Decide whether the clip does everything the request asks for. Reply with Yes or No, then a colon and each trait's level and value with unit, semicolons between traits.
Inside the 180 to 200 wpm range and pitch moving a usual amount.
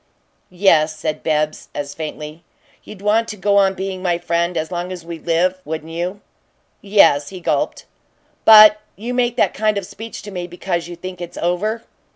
Yes: average, 185 wpm; average, 3.4 semitones